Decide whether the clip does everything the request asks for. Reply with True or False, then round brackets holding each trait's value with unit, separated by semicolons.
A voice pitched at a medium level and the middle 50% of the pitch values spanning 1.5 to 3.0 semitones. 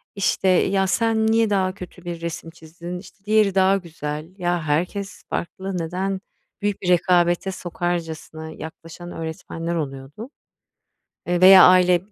True (180 Hz; 2.7 semitones)